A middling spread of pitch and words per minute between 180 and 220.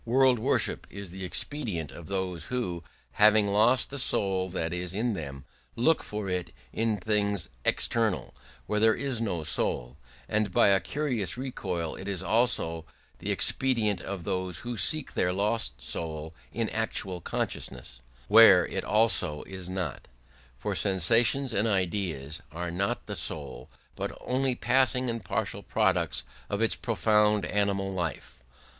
No: average, 4.4 semitones; average, 150 wpm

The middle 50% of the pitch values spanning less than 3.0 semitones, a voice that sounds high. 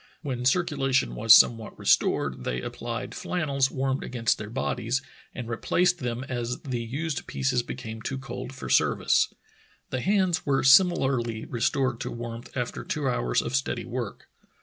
No: narrow, 2.6 semitones; low, 130 Hz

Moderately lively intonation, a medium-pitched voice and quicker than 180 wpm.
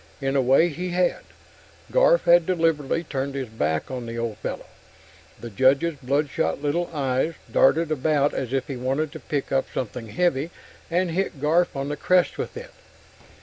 No: average, 4.1 semitones; medium, 145 Hz; average, 175 wpm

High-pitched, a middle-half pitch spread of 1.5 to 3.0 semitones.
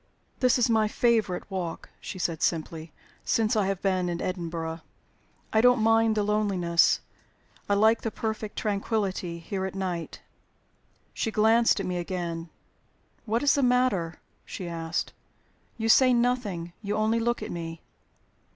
No: high, 200 Hz; average, 4.5 semitones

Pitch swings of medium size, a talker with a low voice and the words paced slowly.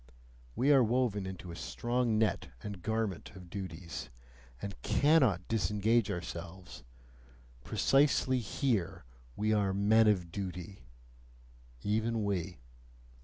Yes: average, 3.7 semitones; low, 100 Hz; slow, 110 wpm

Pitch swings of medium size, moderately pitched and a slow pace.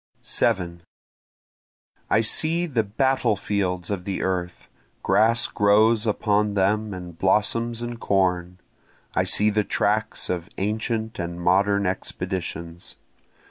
No: average, 3.3 semitones; low, 100 Hz; slow, 115 wpm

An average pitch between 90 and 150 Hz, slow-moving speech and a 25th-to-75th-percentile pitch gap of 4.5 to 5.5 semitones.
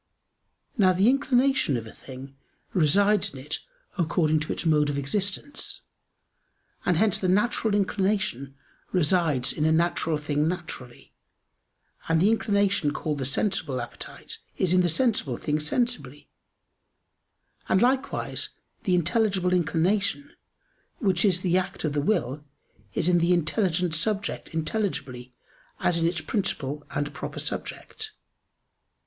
No: medium, 175 Hz; slow, 130 wpm; average, 5.2 semitones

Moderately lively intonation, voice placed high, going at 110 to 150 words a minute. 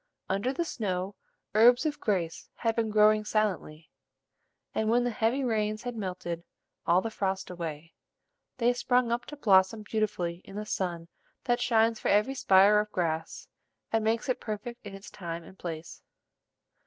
No: average, 3.8 semitones; high, 210 Hz; average, 165 wpm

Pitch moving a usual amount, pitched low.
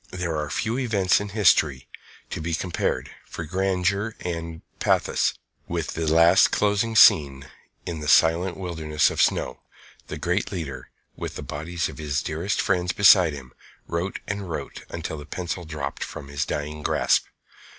Yes: average, 3.7 semitones; very low, 85 Hz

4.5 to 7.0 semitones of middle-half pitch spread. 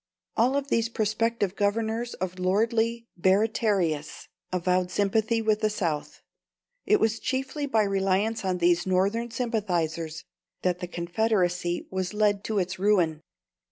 No: average, 3.8 semitones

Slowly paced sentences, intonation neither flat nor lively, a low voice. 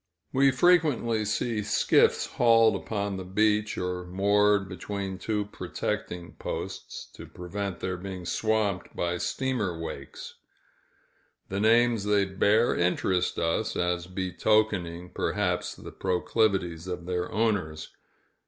Yes: slow, 115 wpm; average, 3.4 semitones; low, 100 Hz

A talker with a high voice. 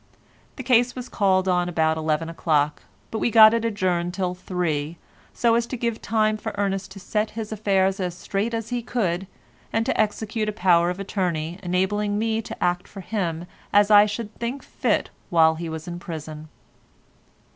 Yes: high, 195 Hz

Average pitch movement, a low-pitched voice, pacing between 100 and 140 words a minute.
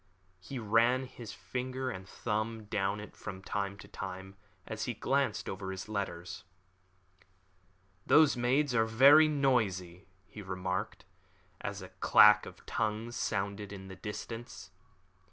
Yes: average, 4.0 semitones; low, 105 Hz; slow, 135 wpm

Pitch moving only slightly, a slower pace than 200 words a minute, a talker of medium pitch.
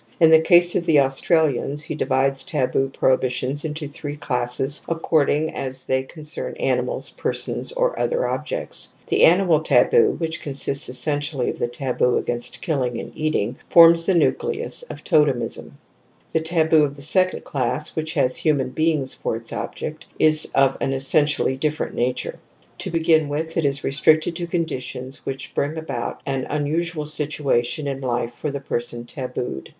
No: average, 3.3 semitones; average, 160 wpm; medium, 145 Hz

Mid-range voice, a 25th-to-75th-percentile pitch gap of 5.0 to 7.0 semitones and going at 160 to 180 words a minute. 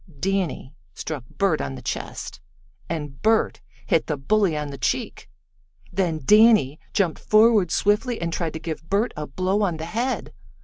Yes: medium, 175 Hz; average, 5.3 semitones; average, 165 wpm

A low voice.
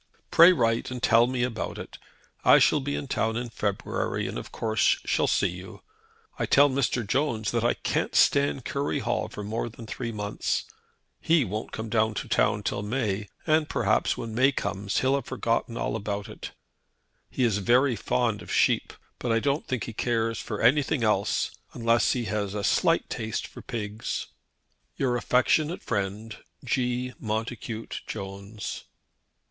Yes: low, 115 Hz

